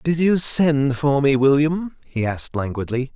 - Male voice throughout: Yes, male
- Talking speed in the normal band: Yes, average, 170 wpm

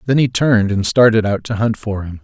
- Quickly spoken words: Yes, fast, 270 wpm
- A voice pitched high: No, low, 110 Hz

